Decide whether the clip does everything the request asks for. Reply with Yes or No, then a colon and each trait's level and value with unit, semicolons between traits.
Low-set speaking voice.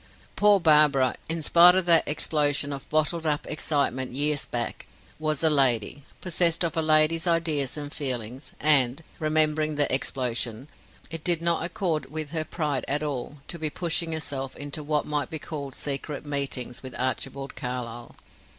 No: medium, 150 Hz